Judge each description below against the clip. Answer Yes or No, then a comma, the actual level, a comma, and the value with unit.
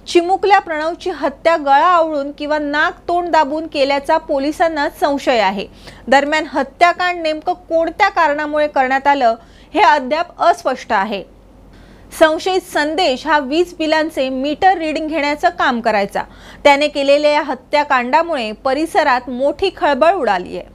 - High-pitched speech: Yes, very high, 310 Hz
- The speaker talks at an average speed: No, slow, 125 wpm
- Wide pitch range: No, average, 3.2 semitones